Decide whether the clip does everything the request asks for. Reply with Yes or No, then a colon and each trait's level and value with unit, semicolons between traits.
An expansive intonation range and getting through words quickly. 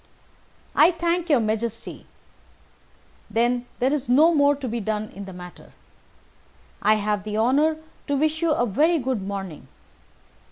No: wide, 6.0 semitones; average, 150 wpm